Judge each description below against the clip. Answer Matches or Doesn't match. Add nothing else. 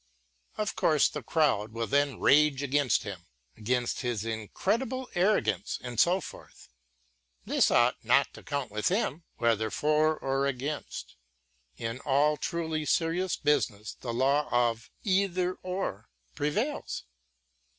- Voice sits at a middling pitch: Matches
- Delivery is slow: Matches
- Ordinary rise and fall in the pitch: Doesn't match